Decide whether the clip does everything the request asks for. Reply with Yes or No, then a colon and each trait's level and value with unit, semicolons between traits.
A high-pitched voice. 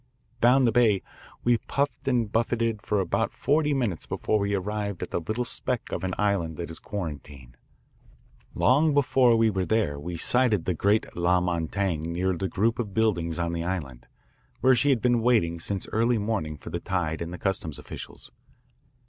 No: low, 100 Hz